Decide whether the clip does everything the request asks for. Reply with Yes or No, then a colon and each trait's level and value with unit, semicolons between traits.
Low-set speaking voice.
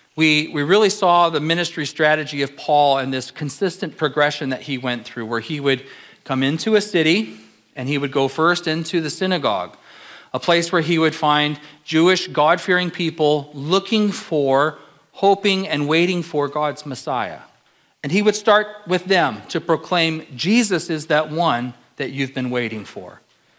No: medium, 155 Hz